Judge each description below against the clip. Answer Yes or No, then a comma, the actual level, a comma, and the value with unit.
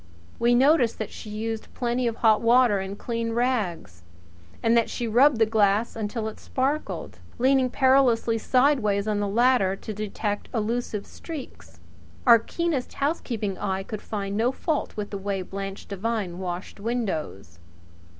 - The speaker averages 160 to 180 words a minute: No, average, 150 wpm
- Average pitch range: Yes, average, 3.5 semitones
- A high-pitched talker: Yes, high, 225 Hz